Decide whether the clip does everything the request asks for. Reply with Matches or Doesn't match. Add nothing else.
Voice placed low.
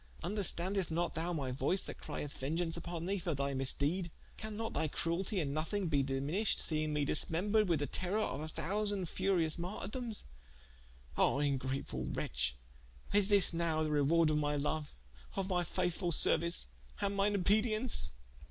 Doesn't match